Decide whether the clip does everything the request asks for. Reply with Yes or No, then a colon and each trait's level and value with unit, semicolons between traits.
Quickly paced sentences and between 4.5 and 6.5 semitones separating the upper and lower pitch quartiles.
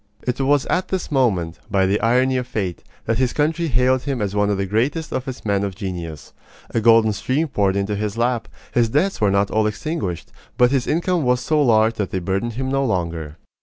Yes: fast, 220 wpm; average, 4.9 semitones